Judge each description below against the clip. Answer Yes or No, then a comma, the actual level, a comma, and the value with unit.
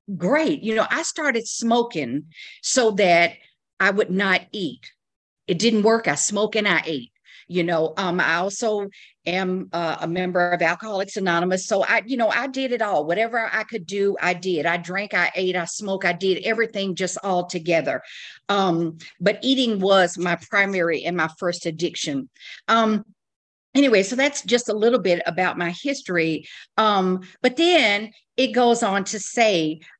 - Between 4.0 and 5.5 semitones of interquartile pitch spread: Yes, average, 4.4 semitones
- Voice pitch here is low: No, high, 195 Hz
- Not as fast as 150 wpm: No, average, 175 wpm